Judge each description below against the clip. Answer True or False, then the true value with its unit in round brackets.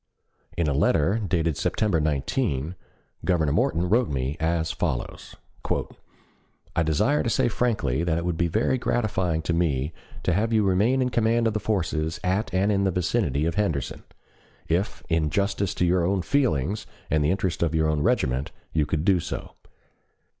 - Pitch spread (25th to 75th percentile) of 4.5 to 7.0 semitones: True (4.8 semitones)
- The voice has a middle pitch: False (85 Hz)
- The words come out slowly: False (175 wpm)